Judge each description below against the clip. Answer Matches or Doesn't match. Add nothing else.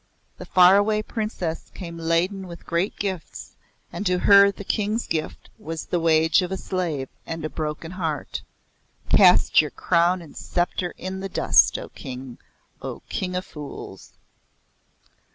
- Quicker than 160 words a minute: Doesn't match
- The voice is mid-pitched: Matches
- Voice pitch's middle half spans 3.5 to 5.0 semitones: Doesn't match